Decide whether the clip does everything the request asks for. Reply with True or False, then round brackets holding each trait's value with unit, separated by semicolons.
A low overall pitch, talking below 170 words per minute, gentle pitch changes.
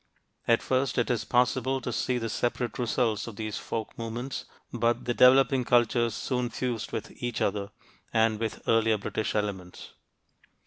True (120 Hz; 160 wpm; 2.0 semitones)